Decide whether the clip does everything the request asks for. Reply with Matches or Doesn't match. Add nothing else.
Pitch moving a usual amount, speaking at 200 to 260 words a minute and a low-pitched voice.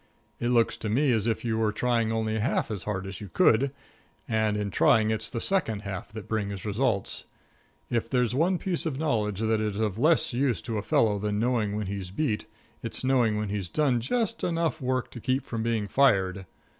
Matches